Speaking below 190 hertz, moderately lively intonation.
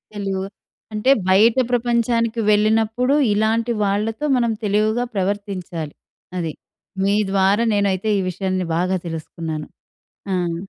No: high, 205 Hz; average, 3.1 semitones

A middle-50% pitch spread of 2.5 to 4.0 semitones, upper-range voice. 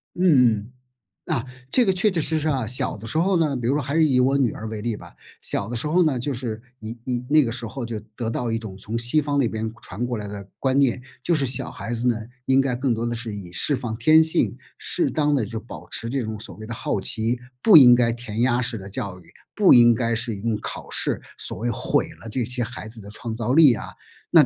No: average, 3.4 semitones; low, 120 Hz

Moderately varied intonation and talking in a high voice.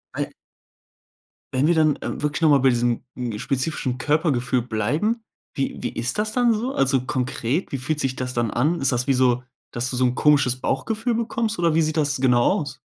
No: average, 4.4 semitones; low, 135 Hz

